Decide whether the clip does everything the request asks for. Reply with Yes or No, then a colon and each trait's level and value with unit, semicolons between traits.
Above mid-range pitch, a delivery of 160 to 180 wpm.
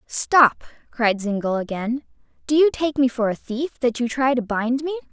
No: very high, 250 Hz; average, 200 wpm